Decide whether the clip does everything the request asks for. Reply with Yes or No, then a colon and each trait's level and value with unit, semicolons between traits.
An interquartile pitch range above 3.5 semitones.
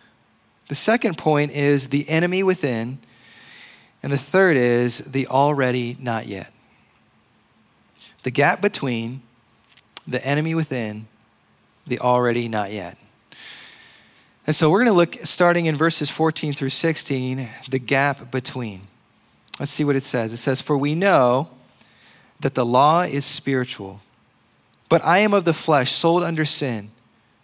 Yes: average, 4.4 semitones